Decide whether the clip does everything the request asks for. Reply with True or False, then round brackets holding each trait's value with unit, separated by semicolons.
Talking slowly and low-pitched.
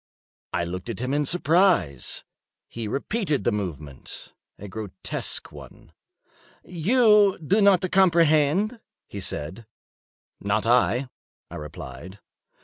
True (105 wpm; 130 Hz)